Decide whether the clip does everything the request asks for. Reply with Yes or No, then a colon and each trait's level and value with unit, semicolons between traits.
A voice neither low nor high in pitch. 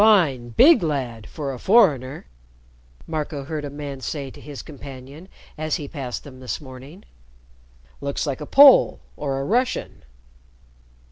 Yes: medium, 145 Hz